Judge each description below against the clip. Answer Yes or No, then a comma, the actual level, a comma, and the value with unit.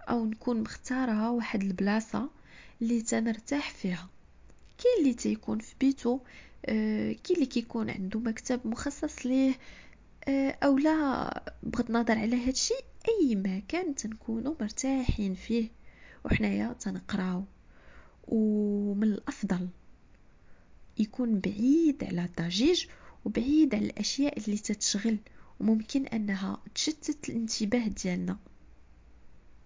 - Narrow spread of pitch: No, average, 4.3 semitones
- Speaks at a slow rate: No, average, 105 wpm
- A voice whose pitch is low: No, high, 230 Hz